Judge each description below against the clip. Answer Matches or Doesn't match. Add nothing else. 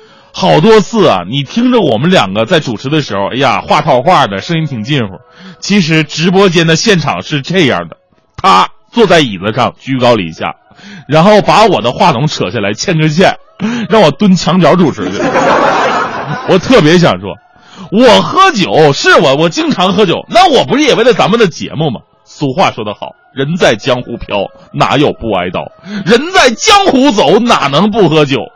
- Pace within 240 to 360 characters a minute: Matches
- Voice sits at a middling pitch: Matches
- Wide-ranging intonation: Matches